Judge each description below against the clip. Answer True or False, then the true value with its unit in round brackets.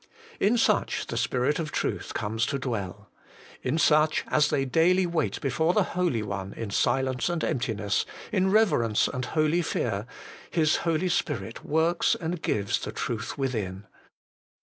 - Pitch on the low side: False (145 Hz)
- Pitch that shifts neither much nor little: False (6.8 semitones)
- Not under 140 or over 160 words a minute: True (150 wpm)